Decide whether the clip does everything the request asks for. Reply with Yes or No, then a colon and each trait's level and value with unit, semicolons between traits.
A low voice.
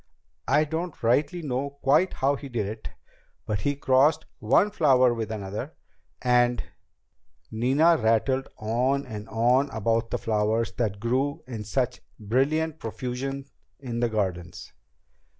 Yes: low, 125 Hz